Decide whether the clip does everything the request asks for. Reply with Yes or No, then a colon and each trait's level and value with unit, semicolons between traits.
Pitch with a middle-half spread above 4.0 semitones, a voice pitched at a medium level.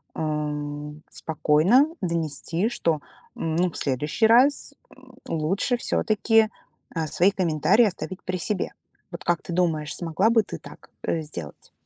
Yes: average, 4.9 semitones; medium, 170 Hz